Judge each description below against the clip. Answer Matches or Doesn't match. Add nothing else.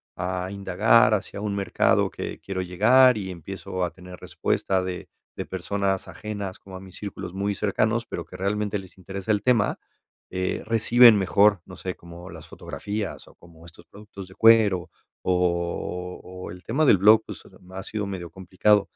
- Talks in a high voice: Doesn't match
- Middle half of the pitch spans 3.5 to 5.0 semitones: Doesn't match